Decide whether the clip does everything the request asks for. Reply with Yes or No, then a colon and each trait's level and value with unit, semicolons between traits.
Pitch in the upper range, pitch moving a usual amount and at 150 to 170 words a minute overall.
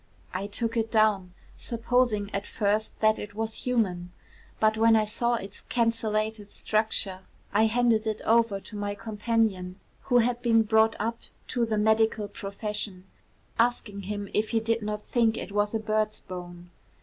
No: high, 215 Hz; narrow, 1.9 semitones; average, 160 wpm